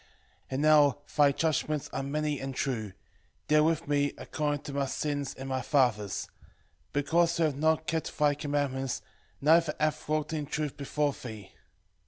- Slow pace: No, average, 165 wpm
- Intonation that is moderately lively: No, narrow, 2.0 semitones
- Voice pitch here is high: No, medium, 145 Hz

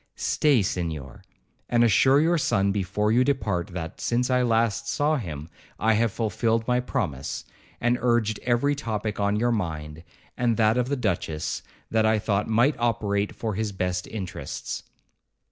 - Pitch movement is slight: No, average, 4.0 semitones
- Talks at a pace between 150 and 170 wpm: Yes, average, 160 wpm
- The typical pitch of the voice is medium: No, low, 110 Hz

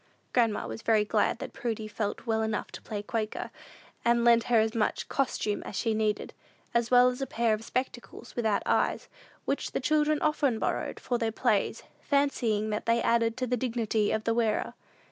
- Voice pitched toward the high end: Yes, high, 230 Hz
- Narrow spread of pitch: Yes, narrow, 2.2 semitones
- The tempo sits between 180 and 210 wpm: Yes, average, 190 wpm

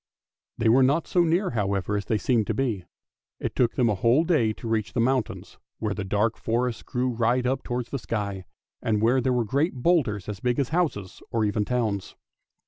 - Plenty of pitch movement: No, average, 3.5 semitones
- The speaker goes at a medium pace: No, fast, 210 wpm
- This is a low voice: Yes, low, 115 Hz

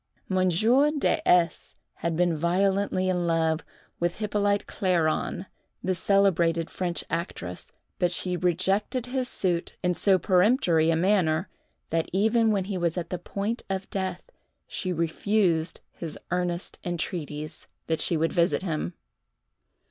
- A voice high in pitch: No, medium, 180 Hz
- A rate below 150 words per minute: Yes, slow, 135 wpm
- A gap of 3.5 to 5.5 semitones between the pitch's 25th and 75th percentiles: No, average, 2.9 semitones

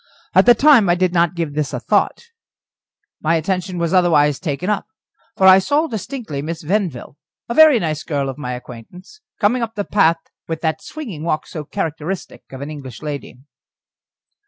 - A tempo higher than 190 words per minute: No, average, 180 wpm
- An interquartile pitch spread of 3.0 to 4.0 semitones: No, average, 5.3 semitones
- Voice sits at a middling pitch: Yes, medium, 170 Hz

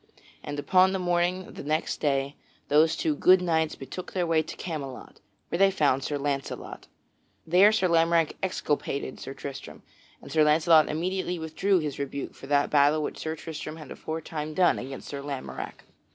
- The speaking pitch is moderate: Yes, medium, 155 Hz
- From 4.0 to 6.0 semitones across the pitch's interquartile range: No, average, 3.5 semitones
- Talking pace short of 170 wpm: No, average, 175 wpm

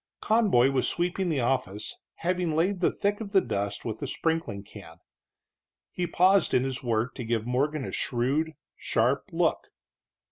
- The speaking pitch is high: No, medium, 140 Hz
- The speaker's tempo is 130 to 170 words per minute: Yes, average, 165 wpm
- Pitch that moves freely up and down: Yes, wide, 7.0 semitones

